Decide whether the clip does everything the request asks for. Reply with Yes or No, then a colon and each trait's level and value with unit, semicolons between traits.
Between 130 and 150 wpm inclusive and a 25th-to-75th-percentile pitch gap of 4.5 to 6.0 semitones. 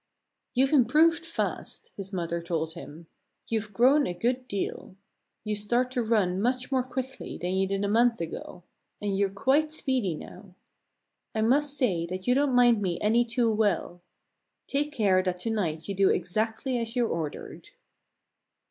No: average, 165 wpm; average, 5.3 semitones